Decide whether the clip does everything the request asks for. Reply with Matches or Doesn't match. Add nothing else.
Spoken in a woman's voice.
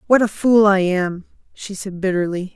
Matches